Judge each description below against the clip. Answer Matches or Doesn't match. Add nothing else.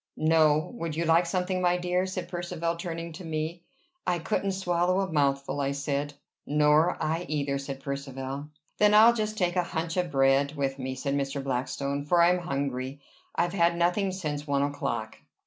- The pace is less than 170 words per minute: Doesn't match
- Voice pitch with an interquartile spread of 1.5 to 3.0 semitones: Doesn't match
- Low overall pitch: Doesn't match